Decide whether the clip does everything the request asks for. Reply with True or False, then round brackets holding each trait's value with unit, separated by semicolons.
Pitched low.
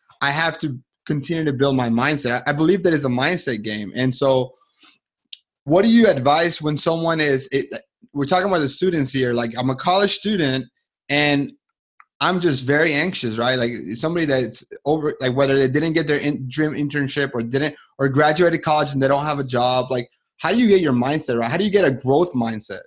False (145 Hz)